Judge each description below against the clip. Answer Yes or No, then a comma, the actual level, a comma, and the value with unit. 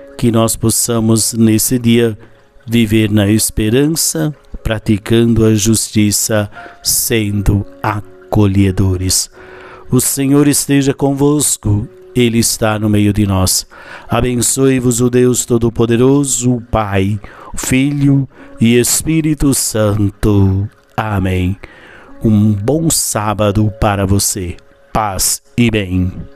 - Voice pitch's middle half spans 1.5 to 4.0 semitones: Yes, average, 3.6 semitones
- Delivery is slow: Yes, slow, 95 wpm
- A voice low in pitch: Yes, low, 115 Hz